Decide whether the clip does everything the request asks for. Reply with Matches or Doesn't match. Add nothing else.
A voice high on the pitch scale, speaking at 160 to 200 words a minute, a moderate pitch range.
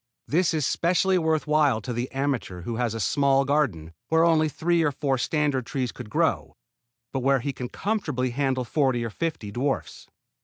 Doesn't match